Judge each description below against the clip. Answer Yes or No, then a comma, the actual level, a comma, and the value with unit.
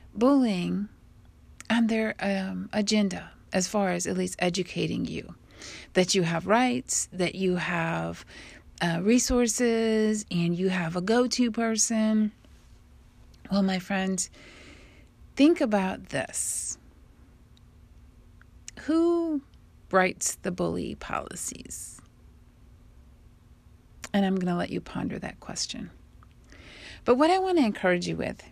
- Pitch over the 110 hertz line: Yes, high, 190 Hz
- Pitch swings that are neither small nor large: Yes, average, 4.7 semitones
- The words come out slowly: Yes, slow, 120 wpm